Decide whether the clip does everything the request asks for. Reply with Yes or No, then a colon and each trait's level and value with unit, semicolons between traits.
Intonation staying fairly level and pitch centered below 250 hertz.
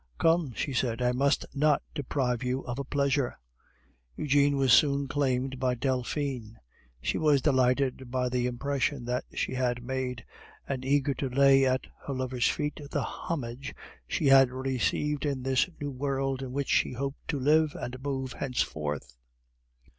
Yes: narrow, 1.9 semitones; low, 135 Hz